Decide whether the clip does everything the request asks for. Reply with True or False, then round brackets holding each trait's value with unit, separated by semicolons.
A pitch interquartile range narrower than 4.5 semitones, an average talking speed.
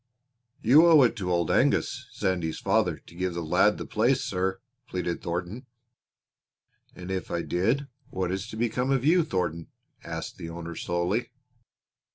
False (5.5 semitones; 160 wpm)